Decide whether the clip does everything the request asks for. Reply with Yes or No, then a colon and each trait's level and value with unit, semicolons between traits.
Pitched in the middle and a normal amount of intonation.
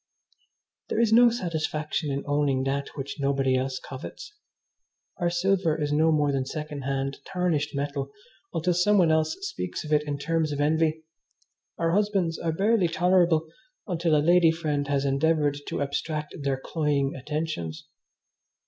Yes: medium, 155 Hz; average, 3.2 semitones